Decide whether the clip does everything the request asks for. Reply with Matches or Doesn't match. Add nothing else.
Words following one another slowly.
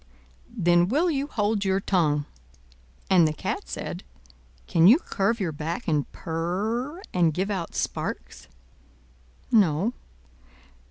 Matches